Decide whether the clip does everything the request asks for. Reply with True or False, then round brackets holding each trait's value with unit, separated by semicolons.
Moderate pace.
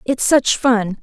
True (175 wpm)